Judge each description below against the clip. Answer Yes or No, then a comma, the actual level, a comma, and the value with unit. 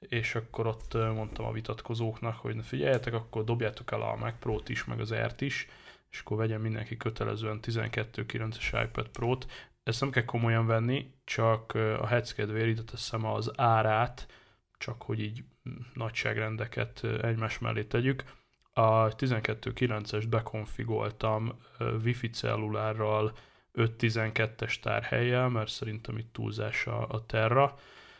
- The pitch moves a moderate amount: No, narrow, 1.6 semitones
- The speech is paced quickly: No, average, 130 wpm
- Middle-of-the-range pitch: No, low, 115 Hz